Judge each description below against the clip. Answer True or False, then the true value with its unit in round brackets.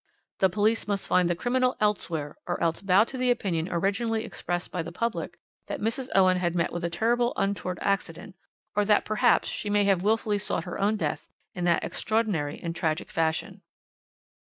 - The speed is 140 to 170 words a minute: False (185 wpm)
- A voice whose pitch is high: True (195 Hz)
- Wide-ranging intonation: False (4.0 semitones)